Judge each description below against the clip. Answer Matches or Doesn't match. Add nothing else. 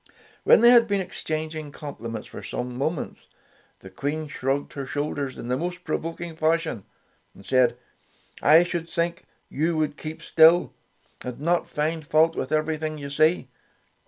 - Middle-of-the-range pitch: Matches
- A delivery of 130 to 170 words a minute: Matches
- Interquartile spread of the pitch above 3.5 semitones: Doesn't match